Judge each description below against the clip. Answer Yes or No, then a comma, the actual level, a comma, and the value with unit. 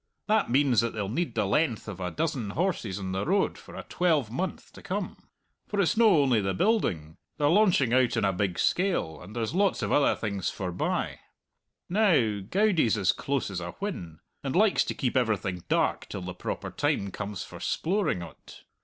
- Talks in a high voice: No, low, 120 Hz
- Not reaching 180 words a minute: No, average, 190 wpm